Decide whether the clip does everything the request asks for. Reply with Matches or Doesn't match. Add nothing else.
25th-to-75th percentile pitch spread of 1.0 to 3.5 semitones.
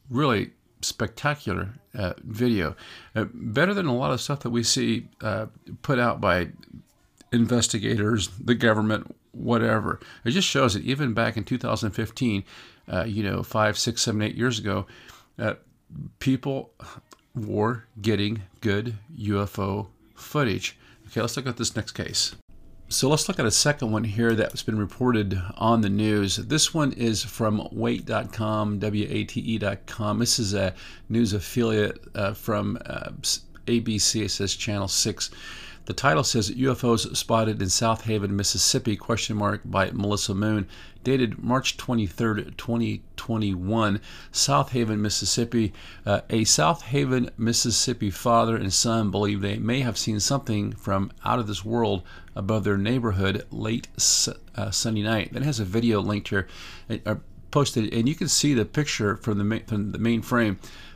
Matches